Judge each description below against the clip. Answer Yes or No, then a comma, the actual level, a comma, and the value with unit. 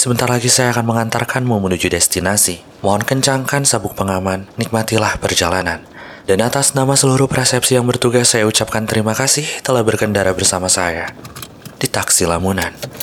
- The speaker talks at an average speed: No, fast, 145 wpm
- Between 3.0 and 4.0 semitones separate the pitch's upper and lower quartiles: No, average, 4.8 semitones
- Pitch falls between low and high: No, low, 110 Hz